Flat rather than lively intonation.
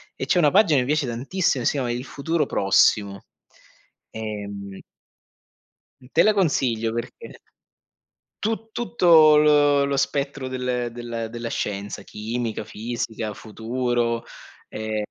No: average, 4.7 semitones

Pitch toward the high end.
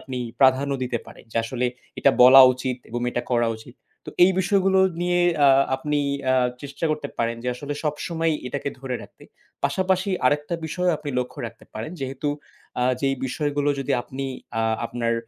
No: low, 135 Hz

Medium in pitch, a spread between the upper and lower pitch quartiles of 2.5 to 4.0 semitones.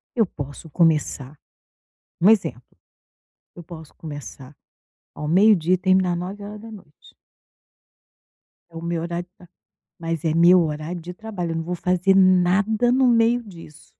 Yes: medium, 175 Hz; average, 3.3 semitones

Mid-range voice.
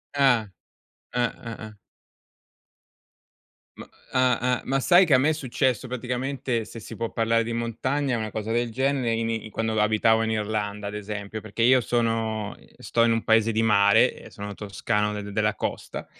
No: low, 115 Hz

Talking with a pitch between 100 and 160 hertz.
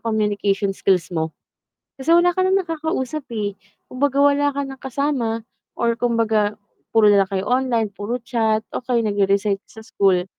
No: high, 225 Hz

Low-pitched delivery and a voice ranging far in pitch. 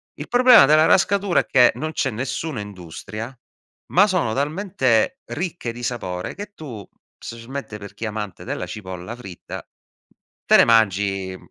Yes: low, 120 Hz; wide, 7.6 semitones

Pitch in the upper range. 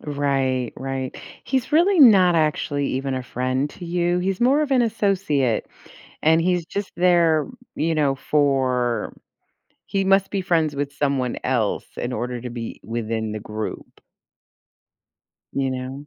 No: medium, 145 Hz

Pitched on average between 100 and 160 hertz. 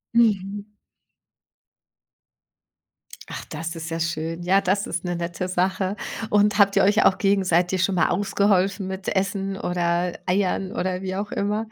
No: high, 190 Hz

